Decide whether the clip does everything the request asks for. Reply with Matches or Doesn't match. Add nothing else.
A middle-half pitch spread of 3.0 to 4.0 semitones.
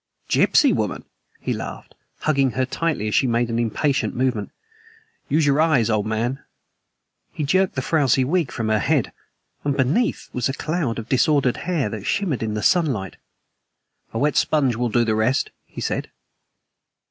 Doesn't match